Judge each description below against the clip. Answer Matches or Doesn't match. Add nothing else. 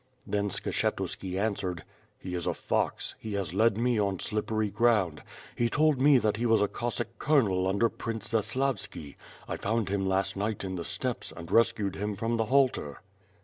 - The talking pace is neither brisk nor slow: Matches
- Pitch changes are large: Doesn't match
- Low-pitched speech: Matches